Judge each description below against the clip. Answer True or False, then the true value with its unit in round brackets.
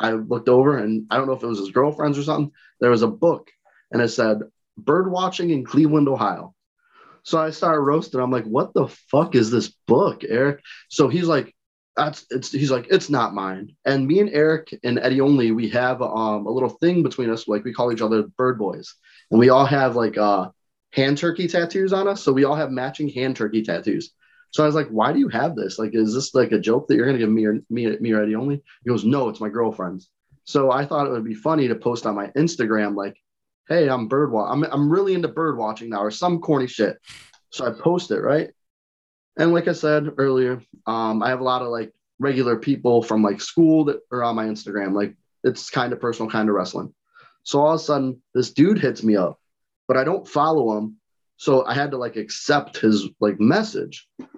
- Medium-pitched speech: False (130 Hz)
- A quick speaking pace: True (230 wpm)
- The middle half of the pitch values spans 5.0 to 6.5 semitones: True (5.3 semitones)